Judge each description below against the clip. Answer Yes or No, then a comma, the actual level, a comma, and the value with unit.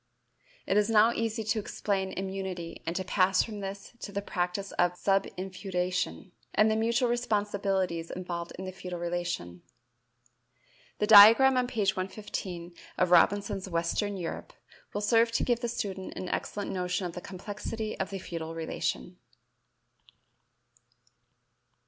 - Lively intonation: No, average, 2.8 semitones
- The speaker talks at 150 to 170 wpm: No, average, 140 wpm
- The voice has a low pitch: No, high, 195 Hz